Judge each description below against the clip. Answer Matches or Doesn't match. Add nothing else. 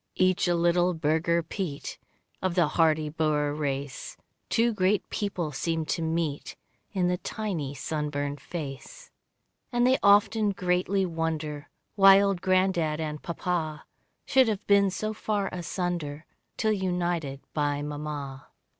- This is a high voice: Doesn't match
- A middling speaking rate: Doesn't match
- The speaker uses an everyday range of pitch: Matches